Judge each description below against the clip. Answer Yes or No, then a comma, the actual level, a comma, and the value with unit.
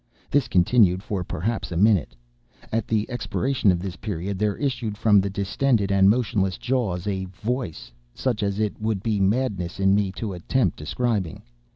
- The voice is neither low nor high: No, low, 100 Hz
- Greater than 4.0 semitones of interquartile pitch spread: No, average, 3.3 semitones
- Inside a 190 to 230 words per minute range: No, average, 165 wpm